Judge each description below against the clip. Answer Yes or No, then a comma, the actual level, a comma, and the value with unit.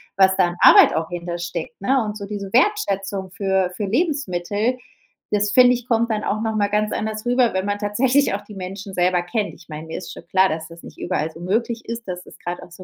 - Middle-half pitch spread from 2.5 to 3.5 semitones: No, average, 3.9 semitones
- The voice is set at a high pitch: Yes, high, 200 Hz